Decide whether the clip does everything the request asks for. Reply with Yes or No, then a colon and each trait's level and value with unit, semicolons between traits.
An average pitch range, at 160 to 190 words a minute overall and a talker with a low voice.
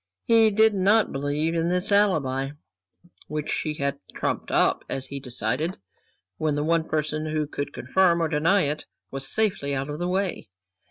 No: average, 4.5 semitones; average, 170 wpm; medium, 155 Hz